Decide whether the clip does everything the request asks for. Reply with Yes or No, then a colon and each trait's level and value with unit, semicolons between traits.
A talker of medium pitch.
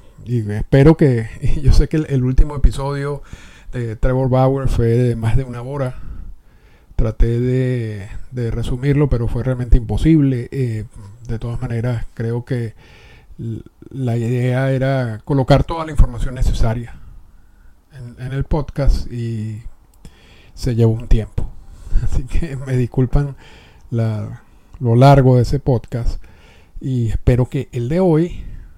No: low, 125 Hz